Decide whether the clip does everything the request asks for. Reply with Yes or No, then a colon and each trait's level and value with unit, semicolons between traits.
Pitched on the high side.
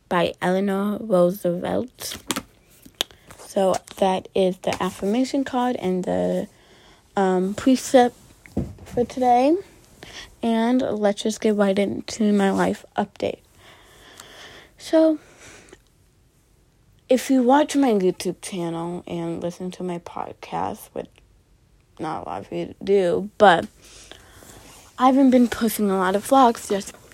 Yes: high, 200 Hz